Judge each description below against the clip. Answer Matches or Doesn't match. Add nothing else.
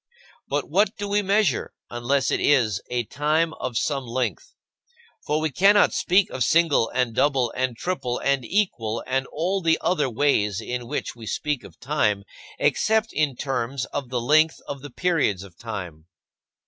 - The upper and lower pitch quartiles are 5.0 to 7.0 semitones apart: Matches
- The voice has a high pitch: Doesn't match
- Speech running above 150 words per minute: Matches